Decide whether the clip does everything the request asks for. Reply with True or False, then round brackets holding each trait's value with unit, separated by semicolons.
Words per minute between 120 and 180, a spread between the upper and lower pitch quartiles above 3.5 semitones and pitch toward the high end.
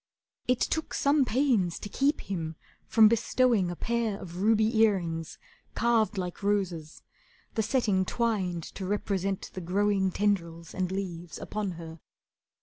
True (140 wpm; 4.1 semitones; 200 Hz)